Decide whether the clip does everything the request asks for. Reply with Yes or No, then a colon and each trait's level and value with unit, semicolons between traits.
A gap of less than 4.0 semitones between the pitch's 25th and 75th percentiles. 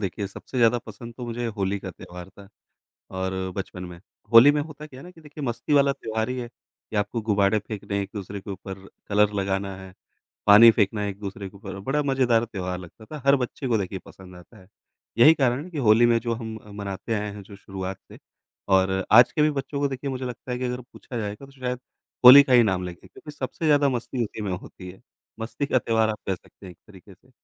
No: average, 4.6 semitones